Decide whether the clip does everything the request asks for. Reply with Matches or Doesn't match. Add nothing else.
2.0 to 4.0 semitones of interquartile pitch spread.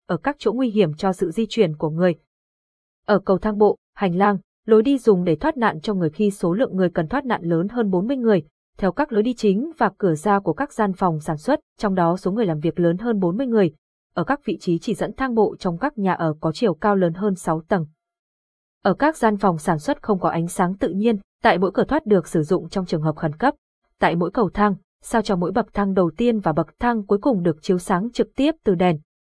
Doesn't match